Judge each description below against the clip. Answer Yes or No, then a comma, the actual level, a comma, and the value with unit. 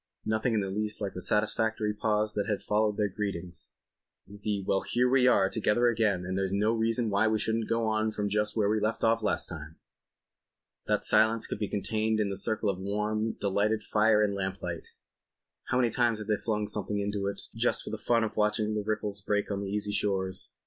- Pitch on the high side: No, low, 105 Hz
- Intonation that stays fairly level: Yes, narrow, 1.6 semitones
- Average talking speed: No, fast, 210 wpm